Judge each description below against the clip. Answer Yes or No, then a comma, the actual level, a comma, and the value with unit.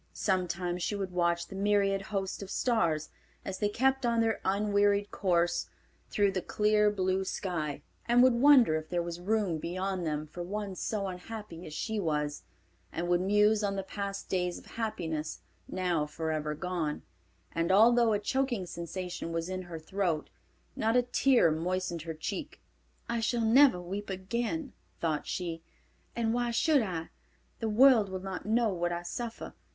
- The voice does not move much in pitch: No, average, 4.1 semitones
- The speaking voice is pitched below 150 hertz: No, high, 190 Hz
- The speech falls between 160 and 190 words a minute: Yes, average, 165 wpm